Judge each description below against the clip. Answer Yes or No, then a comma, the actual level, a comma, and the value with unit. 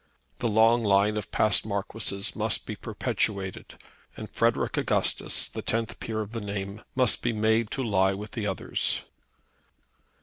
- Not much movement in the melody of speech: Yes, narrow, 2.2 semitones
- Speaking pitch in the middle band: No, low, 105 Hz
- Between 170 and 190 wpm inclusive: No, average, 155 wpm